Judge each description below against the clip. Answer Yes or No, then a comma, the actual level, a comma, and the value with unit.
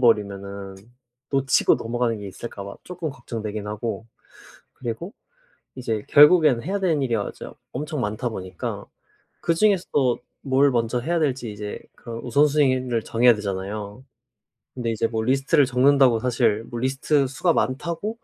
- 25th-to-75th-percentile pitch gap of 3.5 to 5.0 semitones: Yes, average, 4.3 semitones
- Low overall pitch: Yes, low, 125 Hz